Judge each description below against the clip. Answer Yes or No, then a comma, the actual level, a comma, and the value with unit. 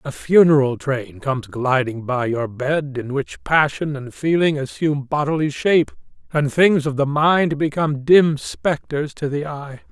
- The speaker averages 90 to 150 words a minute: No, average, 165 wpm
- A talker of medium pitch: Yes, medium, 145 Hz